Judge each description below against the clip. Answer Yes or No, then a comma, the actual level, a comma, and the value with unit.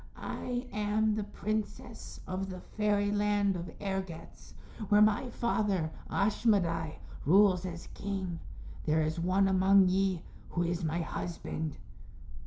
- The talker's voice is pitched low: No, high, 195 Hz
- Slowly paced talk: Yes, slow, 120 wpm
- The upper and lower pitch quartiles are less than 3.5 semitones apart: Yes, average, 3.1 semitones